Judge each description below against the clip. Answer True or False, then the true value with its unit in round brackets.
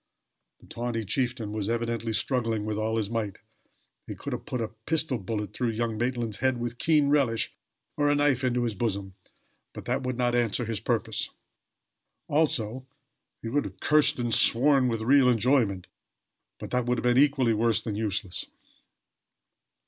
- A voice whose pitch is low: True (120 Hz)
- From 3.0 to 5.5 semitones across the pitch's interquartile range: False (2.6 semitones)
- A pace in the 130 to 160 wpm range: False (170 wpm)